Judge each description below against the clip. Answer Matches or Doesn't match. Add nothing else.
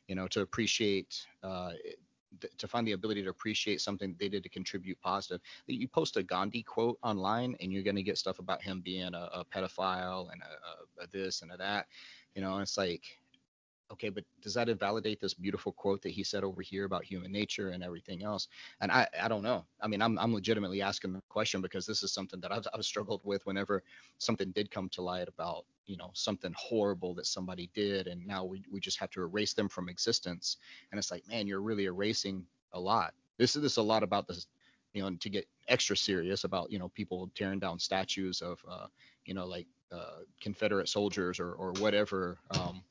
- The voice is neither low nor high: Doesn't match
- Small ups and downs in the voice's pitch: Matches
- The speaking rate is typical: Doesn't match